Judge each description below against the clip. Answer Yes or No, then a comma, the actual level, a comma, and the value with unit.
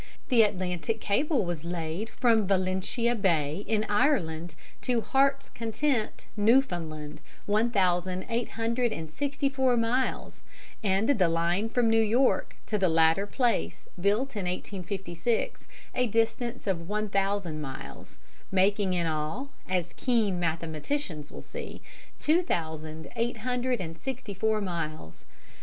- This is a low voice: No, high, 205 Hz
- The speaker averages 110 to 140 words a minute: Yes, slow, 135 wpm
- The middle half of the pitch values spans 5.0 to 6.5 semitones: Yes, wide, 5.5 semitones